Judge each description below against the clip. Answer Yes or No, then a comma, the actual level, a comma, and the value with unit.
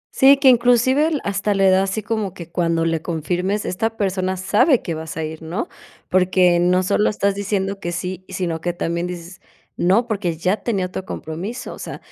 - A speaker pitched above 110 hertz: Yes, medium, 185 Hz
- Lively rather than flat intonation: No, average, 3.2 semitones